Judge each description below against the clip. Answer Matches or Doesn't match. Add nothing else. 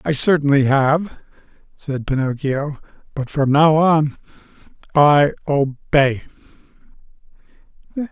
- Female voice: Doesn't match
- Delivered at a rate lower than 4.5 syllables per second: Matches